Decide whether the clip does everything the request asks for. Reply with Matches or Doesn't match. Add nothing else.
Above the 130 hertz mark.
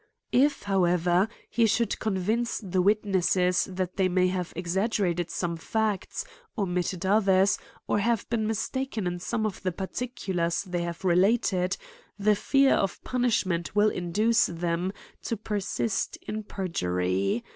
Matches